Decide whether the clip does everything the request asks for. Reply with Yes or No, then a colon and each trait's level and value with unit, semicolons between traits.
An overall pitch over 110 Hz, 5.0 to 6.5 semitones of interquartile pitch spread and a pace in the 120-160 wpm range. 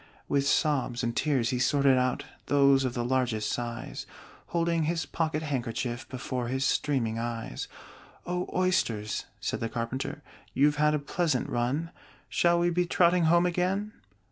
Yes: medium, 140 Hz; wide, 5.6 semitones; average, 150 wpm